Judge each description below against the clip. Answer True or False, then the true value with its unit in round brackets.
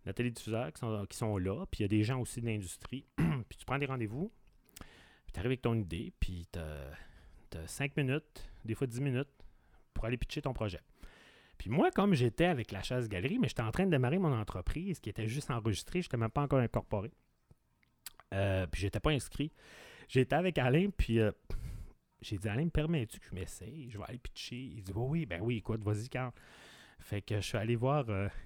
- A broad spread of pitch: True (5.7 semitones)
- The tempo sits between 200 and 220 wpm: True (215 wpm)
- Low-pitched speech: True (115 Hz)